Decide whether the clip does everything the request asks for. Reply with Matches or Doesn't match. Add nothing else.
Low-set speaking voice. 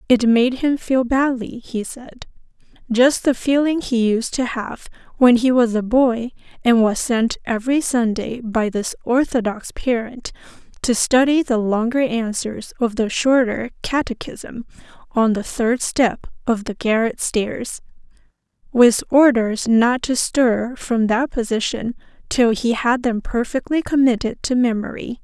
Doesn't match